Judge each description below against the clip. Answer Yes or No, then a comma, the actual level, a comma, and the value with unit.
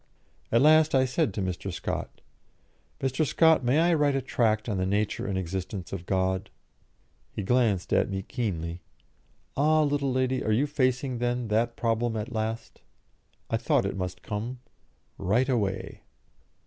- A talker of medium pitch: No, low, 115 Hz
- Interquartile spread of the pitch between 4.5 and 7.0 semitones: Yes, average, 5.1 semitones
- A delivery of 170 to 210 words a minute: No, average, 160 wpm